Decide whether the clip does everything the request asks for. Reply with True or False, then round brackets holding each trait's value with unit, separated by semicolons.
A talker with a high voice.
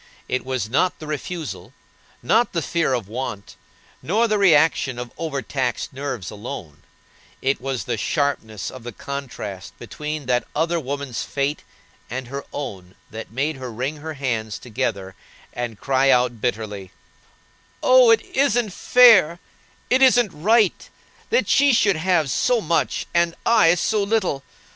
False (140 Hz)